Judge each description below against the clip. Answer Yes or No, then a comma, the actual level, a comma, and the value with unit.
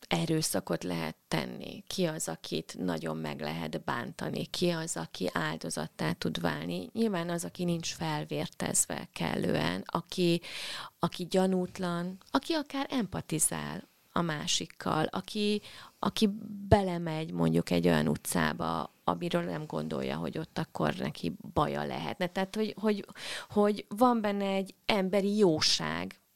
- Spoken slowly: No, average, 125 wpm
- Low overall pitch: No, medium, 170 Hz